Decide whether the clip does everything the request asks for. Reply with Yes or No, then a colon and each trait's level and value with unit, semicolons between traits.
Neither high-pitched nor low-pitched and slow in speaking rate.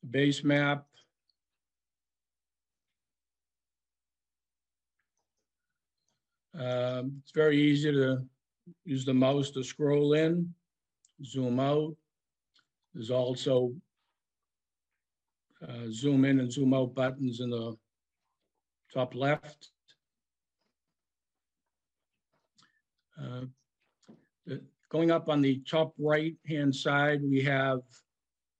No: low, 130 Hz; slow, 80 wpm